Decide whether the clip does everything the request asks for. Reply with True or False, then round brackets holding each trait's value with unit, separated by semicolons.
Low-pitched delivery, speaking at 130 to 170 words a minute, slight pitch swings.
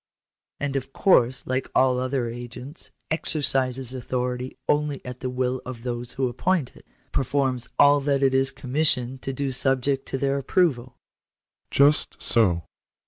True (130 Hz; 160 wpm; 1.8 semitones)